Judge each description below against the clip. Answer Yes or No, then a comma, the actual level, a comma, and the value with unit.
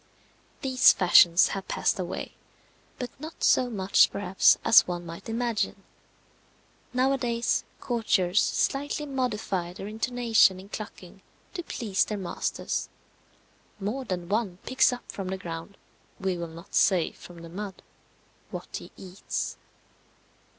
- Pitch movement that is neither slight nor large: Yes, average, 5.0 semitones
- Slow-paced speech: Yes, slow, 130 wpm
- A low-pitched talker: No, high, 200 Hz